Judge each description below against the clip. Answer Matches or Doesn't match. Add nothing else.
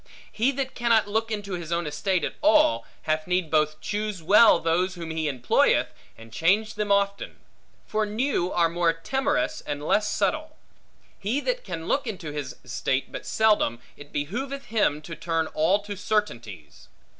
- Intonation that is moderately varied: Doesn't match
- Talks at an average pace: Matches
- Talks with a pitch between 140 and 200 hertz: Matches